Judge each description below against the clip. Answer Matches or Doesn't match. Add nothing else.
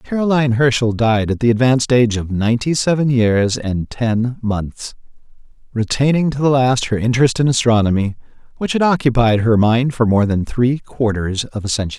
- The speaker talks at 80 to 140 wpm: Doesn't match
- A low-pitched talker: Matches